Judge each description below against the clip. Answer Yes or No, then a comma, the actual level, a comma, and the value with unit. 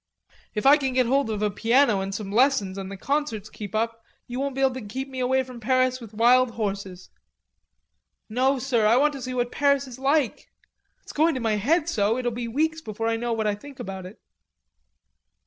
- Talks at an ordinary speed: No, fast, 215 wpm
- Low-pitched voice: No, high, 245 Hz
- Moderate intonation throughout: Yes, average, 3.9 semitones